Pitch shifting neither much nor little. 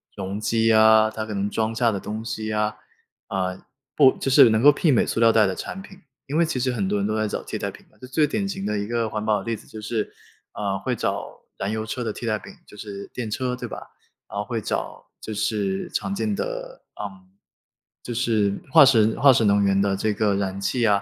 Yes: average, 3.5 semitones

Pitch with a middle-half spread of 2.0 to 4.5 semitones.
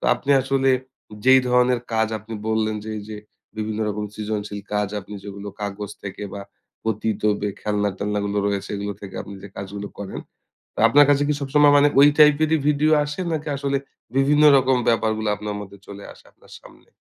No: average, 4.9 semitones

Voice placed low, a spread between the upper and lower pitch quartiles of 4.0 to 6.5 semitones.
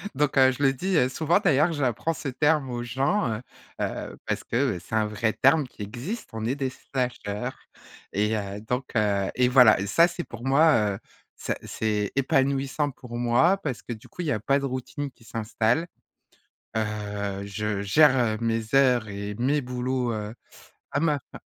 Yes: low, 125 Hz; average, 4.3 semitones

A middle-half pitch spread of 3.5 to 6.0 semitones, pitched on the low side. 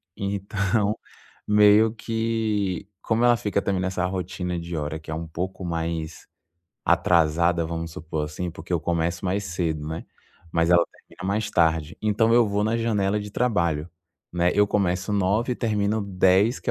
Yes: average, 3.8 semitones; very low, 95 Hz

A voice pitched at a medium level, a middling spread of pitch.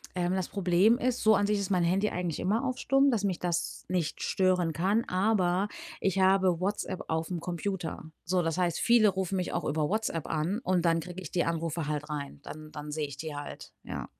Yes: medium, 180 Hz; average, 3.1 semitones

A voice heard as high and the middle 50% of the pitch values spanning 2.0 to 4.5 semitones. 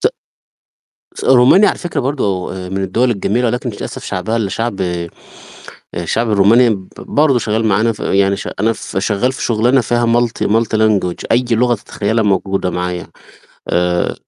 No: low, 110 Hz; average, 3.7 semitones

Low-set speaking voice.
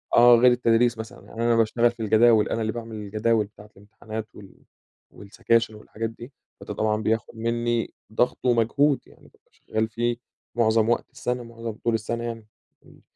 Yes: low, 115 Hz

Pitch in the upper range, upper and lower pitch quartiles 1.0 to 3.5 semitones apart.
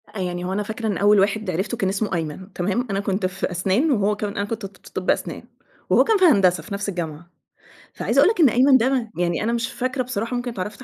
No: high, 205 Hz; average, 4.1 semitones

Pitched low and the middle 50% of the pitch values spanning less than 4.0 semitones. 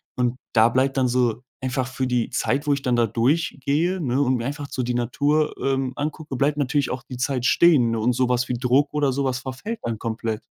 Yes: low, 130 Hz; average, 2.7 semitones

